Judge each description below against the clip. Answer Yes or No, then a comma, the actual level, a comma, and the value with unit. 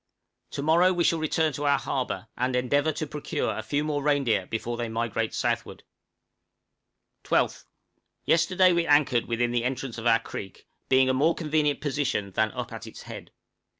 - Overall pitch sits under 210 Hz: Yes, low, 135 Hz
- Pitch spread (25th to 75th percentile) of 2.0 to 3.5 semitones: No, average, 4.5 semitones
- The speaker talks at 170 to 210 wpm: Yes, average, 175 wpm